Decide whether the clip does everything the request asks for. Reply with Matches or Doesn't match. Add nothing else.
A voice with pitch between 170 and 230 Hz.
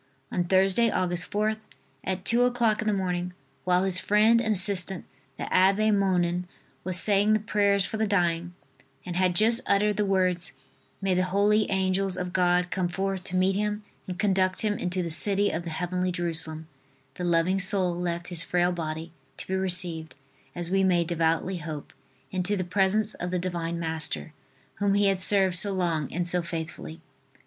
Matches